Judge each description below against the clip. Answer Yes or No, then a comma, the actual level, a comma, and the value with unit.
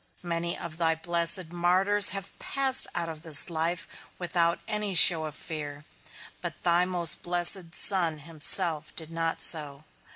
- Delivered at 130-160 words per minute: Yes, average, 150 wpm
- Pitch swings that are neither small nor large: No, narrow, 1.8 semitones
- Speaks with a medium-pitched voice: Yes, medium, 170 Hz